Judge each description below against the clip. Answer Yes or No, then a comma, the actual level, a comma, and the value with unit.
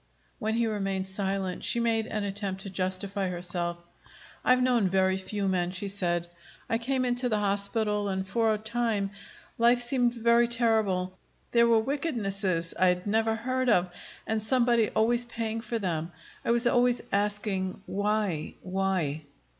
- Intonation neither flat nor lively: Yes, average, 3.6 semitones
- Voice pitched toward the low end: No, high, 210 Hz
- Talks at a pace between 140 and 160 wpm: Yes, average, 155 wpm